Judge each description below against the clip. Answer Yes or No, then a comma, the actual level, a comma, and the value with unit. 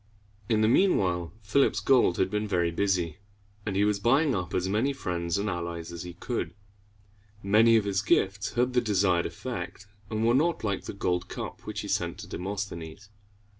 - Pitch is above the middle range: No, low, 100 Hz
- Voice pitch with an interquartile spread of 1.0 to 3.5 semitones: No, average, 4.0 semitones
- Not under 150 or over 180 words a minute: No, average, 190 wpm